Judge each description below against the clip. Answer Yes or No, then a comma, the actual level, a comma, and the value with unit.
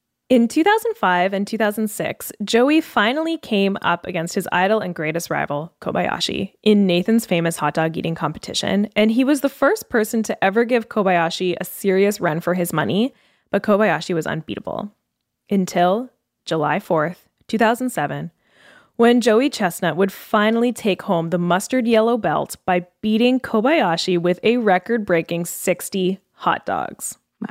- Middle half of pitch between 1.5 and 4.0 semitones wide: No, average, 4.8 semitones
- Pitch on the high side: Yes, high, 200 Hz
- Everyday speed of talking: Yes, average, 145 wpm